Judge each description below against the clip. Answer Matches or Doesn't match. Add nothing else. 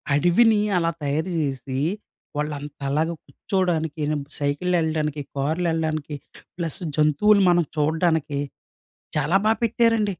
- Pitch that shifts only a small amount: Doesn't match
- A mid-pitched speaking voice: Matches